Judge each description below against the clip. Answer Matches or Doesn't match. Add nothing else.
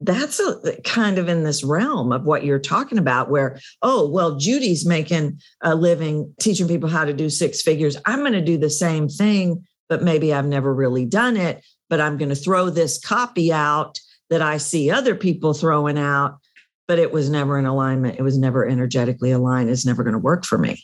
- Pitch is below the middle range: Doesn't match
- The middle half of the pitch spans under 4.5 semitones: Matches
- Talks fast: Matches